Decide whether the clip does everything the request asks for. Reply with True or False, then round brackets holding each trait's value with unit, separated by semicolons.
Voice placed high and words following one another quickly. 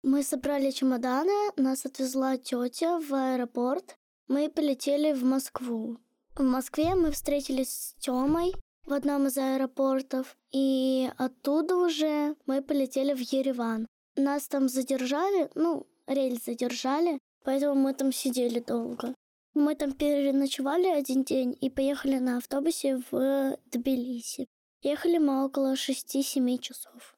False (270 Hz; 125 wpm)